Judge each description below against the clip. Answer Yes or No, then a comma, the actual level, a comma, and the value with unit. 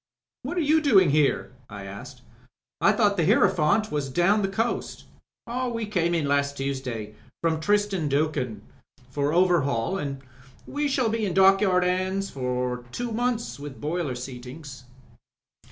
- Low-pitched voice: No, medium, 165 Hz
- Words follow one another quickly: No, average, 155 wpm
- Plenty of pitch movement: Yes, wide, 7.2 semitones